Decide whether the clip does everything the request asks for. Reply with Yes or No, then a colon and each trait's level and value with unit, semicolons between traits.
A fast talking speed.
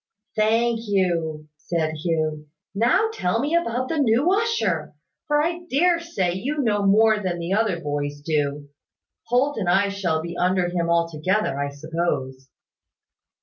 No: average, 150 wpm